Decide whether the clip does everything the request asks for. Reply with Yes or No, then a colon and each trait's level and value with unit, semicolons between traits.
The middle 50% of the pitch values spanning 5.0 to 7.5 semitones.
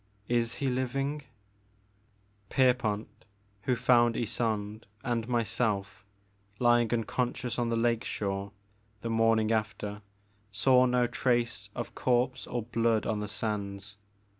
No: narrow, 2.5 semitones